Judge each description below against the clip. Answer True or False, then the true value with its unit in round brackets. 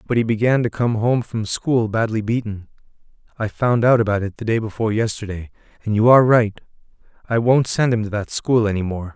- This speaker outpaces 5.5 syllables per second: True (5.8 syllables/s)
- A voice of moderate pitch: False (110 Hz)